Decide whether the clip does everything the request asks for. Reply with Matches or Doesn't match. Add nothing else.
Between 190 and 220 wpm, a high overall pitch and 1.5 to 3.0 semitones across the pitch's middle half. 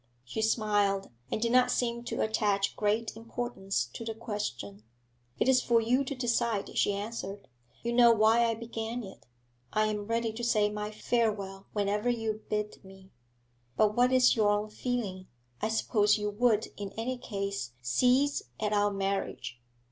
Doesn't match